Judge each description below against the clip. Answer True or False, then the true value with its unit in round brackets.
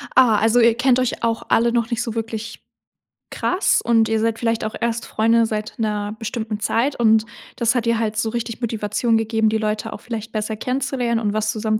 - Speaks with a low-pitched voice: False (225 Hz)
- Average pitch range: False (1.3 semitones)